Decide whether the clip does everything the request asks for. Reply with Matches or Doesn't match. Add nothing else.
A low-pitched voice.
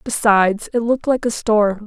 Doesn't match